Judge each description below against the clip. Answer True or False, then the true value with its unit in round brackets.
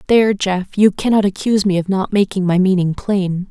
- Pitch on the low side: False (195 Hz)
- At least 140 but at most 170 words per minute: False (205 wpm)